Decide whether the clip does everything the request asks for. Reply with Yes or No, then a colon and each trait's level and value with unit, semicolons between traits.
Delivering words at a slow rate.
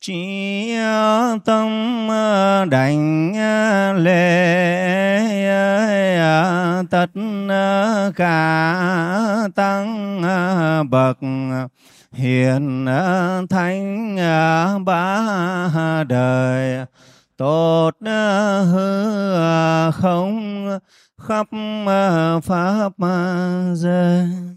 Yes: slow, 45 wpm